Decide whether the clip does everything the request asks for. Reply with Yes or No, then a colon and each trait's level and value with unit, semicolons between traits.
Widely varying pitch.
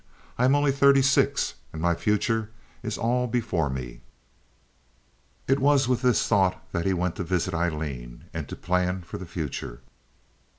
Yes: wide, 7.0 semitones